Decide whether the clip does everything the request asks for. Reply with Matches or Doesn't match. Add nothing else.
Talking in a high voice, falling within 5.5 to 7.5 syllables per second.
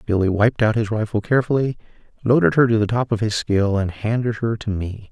Doesn't match